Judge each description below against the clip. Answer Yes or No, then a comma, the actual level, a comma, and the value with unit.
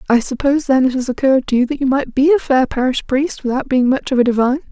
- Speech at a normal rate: No, fast, 280 wpm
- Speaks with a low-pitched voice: No, very high, 265 Hz